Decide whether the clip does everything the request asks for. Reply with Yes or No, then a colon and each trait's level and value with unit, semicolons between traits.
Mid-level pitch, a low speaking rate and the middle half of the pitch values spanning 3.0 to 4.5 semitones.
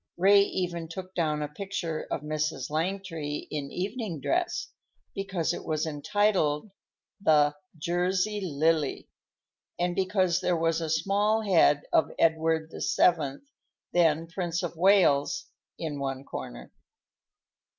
Yes: medium, 165 Hz; slow, 120 wpm; average, 3.7 semitones